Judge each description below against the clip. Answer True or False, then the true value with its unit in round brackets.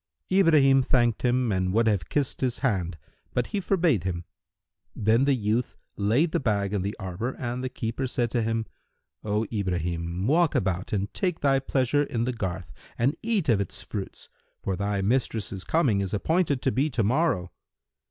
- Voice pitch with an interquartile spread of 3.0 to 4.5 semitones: False (5.3 semitones)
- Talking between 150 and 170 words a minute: False (180 wpm)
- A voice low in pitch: True (115 Hz)